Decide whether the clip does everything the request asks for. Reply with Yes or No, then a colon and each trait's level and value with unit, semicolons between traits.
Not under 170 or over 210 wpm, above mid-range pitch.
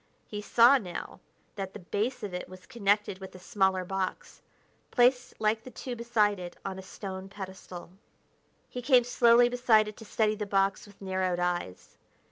Yes: average, 175 wpm; high, 205 Hz